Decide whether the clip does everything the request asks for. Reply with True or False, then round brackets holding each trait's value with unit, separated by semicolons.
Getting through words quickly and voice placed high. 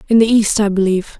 True (250 wpm; 210 Hz)